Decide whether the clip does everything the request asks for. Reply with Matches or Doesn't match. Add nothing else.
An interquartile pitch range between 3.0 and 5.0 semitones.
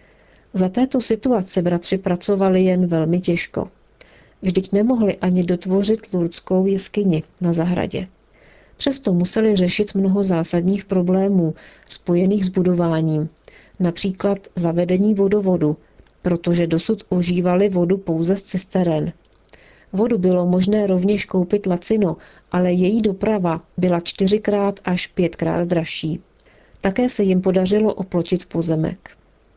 Doesn't match